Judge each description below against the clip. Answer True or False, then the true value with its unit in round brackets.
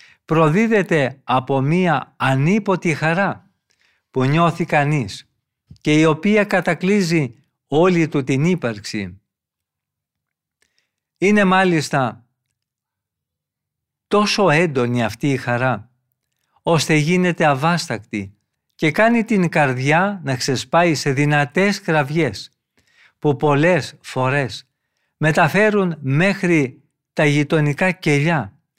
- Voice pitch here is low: False (150 Hz)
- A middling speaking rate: False (90 wpm)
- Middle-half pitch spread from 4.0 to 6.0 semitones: True (5.2 semitones)